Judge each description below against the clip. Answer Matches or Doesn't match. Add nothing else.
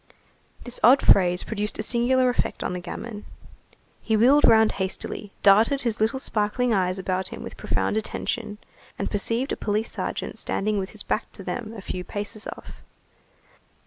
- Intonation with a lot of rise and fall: Doesn't match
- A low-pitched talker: Doesn't match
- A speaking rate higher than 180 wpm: Doesn't match